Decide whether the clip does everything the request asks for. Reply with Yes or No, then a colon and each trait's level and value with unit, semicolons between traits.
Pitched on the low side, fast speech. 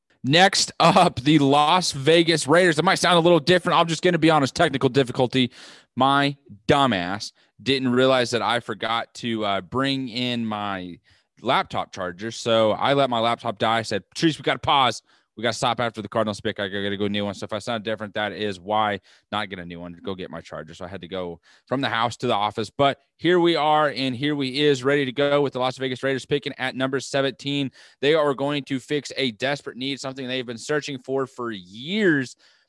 Yes: low, 130 Hz; fast, 230 wpm